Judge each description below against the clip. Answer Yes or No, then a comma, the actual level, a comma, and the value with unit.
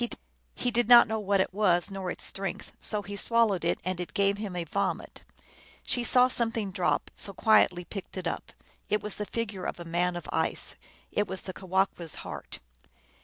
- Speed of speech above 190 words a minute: Yes, fast, 205 wpm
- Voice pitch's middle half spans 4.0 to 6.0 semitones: No, average, 3.0 semitones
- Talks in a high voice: Yes, high, 195 Hz